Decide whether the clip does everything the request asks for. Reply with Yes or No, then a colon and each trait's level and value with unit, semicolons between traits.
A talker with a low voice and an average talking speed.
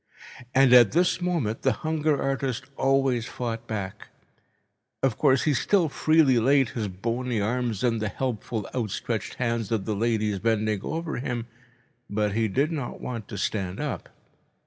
Yes: low, 120 Hz; average, 155 wpm